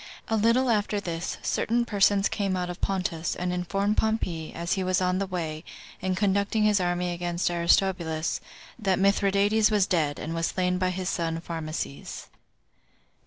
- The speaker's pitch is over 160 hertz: Yes, medium, 185 Hz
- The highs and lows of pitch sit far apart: No, average, 2.8 semitones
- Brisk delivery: No, average, 165 wpm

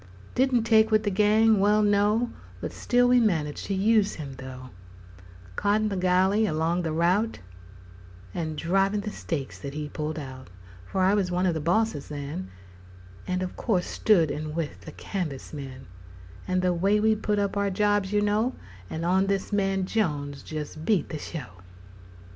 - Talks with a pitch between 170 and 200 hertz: Yes, medium, 185 Hz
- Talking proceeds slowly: No, average, 170 wpm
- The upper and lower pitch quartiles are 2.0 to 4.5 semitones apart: No, average, 5.2 semitones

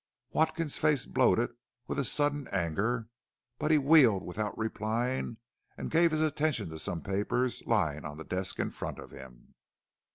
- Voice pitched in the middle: No, low, 115 Hz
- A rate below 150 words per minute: No, average, 160 wpm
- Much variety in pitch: Yes, wide, 7.4 semitones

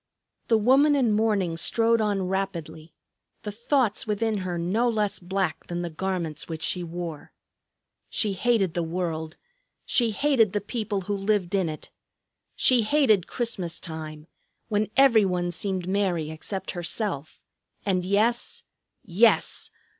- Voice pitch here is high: Yes, high, 195 Hz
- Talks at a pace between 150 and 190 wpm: No, average, 140 wpm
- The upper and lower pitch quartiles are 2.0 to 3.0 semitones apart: No, average, 4.1 semitones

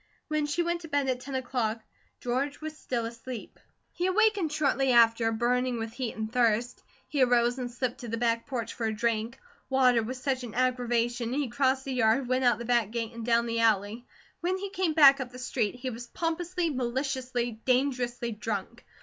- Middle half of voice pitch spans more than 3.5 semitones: No, average, 2.8 semitones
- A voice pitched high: Yes, high, 245 Hz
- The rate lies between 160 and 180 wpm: No, average, 200 wpm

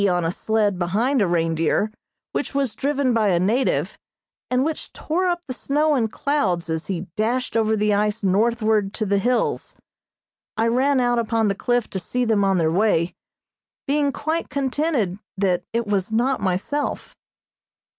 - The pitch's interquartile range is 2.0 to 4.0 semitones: No, average, 5.1 semitones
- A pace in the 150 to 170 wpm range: Yes, average, 165 wpm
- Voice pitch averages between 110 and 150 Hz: No, high, 220 Hz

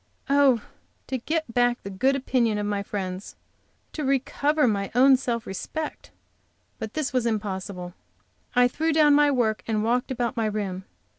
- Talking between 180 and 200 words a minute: No, average, 160 wpm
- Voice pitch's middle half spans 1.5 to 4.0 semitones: No, average, 4.7 semitones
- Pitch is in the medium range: No, high, 240 Hz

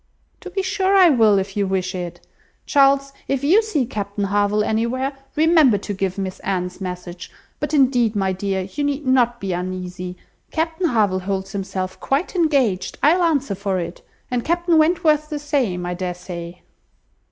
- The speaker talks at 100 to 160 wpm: No, average, 170 wpm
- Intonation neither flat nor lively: No, wide, 7.7 semitones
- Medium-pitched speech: No, high, 220 Hz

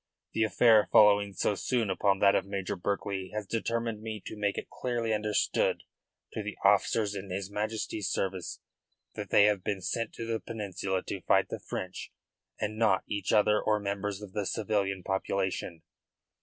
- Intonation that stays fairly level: Yes, narrow, 1.8 semitones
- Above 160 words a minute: Yes, average, 170 wpm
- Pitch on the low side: Yes, low, 105 Hz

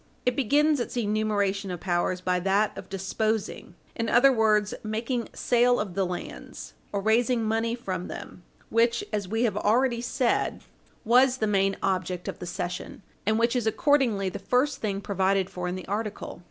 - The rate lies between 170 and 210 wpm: Yes, average, 175 wpm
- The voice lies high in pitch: Yes, high, 215 Hz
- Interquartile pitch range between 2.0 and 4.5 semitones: Yes, average, 3.7 semitones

